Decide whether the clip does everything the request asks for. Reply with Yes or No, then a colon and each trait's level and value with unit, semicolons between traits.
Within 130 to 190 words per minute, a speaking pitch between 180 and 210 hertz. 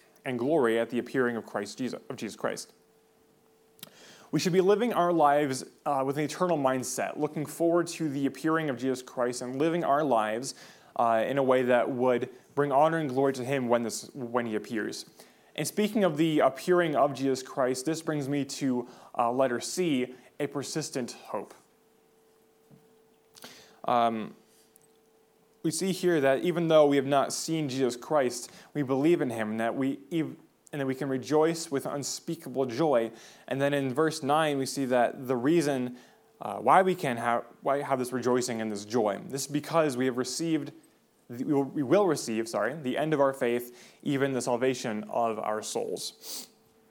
No: average, 180 wpm; low, 135 Hz